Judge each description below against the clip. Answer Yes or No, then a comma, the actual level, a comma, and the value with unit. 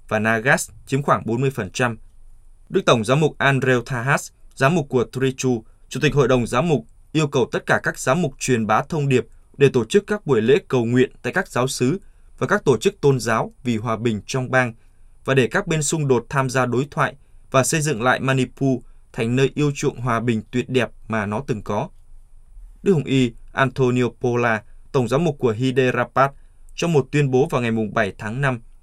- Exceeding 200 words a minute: Yes, average, 210 wpm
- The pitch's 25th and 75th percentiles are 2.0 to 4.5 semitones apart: Yes, average, 3.3 semitones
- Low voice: Yes, low, 130 Hz